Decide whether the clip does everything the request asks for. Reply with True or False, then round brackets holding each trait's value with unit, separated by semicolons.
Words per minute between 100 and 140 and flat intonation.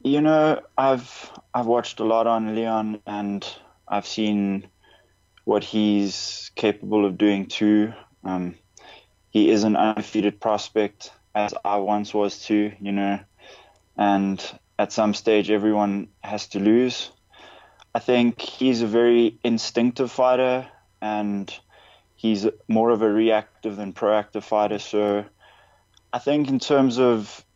True (135 wpm; 2.3 semitones)